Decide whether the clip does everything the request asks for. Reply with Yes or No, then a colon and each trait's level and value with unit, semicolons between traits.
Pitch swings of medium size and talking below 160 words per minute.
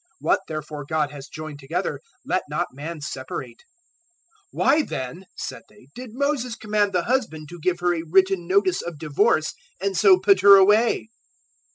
No: average, 4.8 semitones; average, 170 wpm